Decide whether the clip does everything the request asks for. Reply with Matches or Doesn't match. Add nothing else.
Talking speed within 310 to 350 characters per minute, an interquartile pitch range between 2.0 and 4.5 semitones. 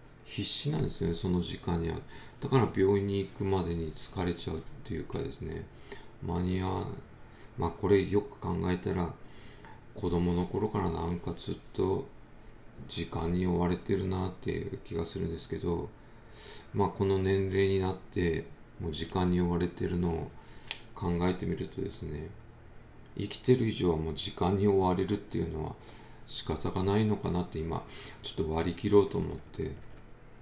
Matches